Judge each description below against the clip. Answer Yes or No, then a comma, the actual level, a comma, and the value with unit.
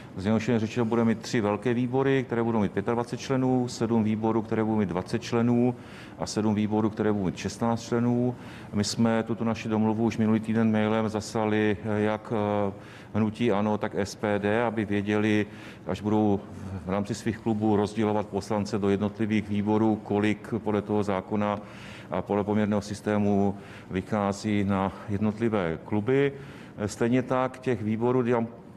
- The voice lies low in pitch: Yes, low, 110 Hz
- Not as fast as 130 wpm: No, average, 150 wpm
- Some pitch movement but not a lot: No, narrow, 2.0 semitones